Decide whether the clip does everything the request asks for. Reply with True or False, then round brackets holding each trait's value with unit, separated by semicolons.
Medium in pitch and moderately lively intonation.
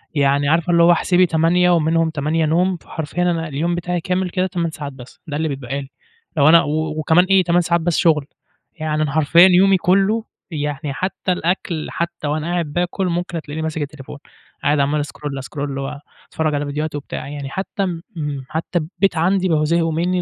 True (160 Hz; 3.1 semitones)